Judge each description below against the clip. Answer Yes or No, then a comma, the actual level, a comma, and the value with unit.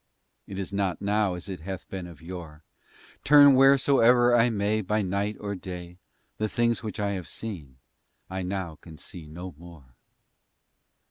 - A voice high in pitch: No, very low, 95 Hz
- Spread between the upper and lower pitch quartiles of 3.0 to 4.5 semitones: Yes, average, 3.6 semitones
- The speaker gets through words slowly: No, average, 160 wpm